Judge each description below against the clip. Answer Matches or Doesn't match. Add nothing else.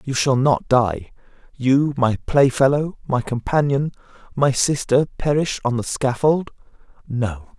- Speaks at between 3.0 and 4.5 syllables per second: Matches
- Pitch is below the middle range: Matches